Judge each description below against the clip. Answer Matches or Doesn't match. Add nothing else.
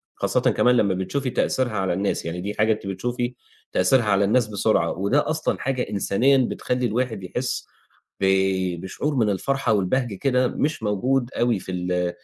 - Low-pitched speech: Matches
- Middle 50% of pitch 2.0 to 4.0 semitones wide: Doesn't match